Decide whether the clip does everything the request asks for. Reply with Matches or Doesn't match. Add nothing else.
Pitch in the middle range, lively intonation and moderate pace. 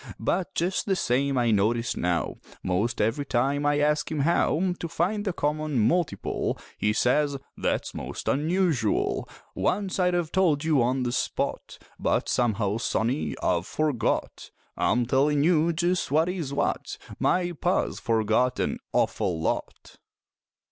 Matches